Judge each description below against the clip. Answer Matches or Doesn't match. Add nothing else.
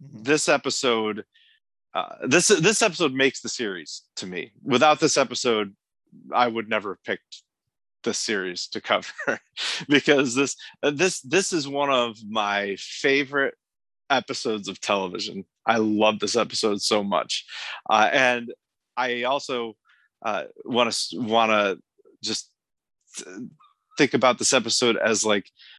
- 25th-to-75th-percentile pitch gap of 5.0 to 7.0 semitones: Matches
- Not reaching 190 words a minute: Matches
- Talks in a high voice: Doesn't match